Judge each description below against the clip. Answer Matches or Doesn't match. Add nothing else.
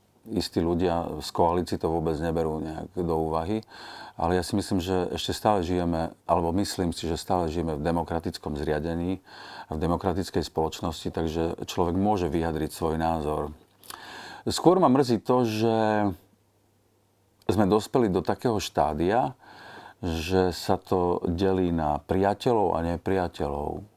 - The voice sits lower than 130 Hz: Matches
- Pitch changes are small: Doesn't match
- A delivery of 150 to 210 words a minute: Doesn't match